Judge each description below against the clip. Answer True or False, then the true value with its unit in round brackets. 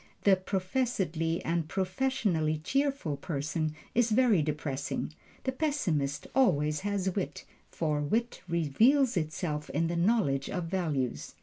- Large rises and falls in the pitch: True (6.3 semitones)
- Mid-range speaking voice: True (170 Hz)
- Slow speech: True (120 wpm)